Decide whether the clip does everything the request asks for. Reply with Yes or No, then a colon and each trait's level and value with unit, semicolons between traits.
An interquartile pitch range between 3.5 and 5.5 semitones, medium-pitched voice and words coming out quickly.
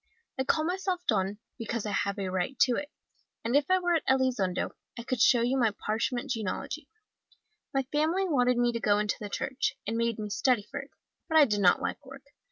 No: average, 5.1 semitones; high, 245 Hz; fast, 215 wpm